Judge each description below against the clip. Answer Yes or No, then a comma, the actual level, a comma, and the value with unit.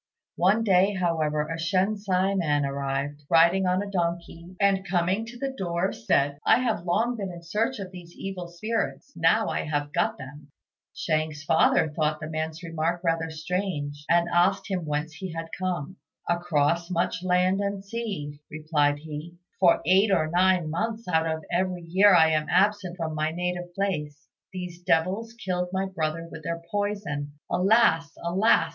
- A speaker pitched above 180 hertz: No, medium, 175 Hz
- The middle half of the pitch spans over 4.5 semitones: No, average, 3.3 semitones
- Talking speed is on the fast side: No, average, 165 wpm